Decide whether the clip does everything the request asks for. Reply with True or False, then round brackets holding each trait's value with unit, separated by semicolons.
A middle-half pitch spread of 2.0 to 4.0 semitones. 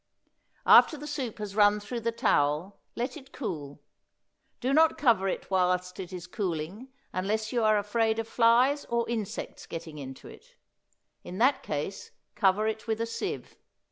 False (4.4 semitones)